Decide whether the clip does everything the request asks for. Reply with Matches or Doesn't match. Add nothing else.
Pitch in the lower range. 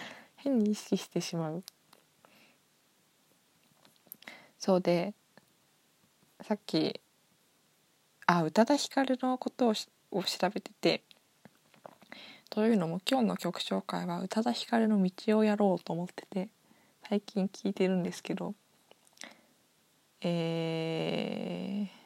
Doesn't match